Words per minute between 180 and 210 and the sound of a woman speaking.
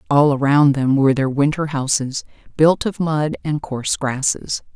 No: average, 165 wpm; female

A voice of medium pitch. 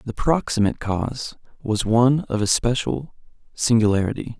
No: low, 115 Hz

